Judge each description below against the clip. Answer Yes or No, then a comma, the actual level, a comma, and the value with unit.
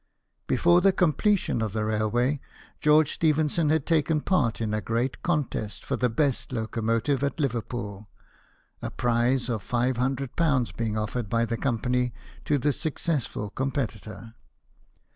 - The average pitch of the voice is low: Yes, low, 125 Hz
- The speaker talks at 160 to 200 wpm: No, average, 140 wpm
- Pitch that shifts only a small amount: No, average, 4.7 semitones